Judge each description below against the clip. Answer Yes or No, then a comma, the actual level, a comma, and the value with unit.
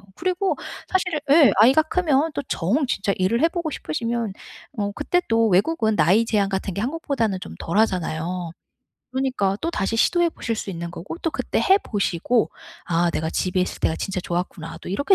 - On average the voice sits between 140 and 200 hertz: No, high, 220 Hz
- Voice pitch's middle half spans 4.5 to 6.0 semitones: No, wide, 8.2 semitones